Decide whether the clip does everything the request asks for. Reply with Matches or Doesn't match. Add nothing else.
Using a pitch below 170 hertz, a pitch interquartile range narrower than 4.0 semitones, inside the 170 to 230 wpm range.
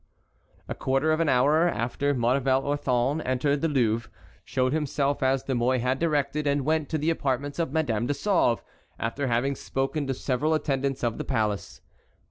Matches